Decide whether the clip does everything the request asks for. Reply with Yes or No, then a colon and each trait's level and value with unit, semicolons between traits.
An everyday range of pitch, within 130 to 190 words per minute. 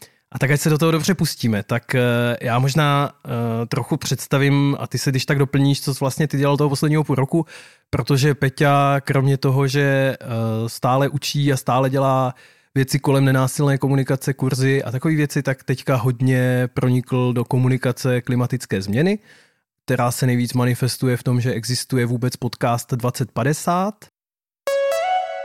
No: narrow, 2.3 semitones; average, 155 wpm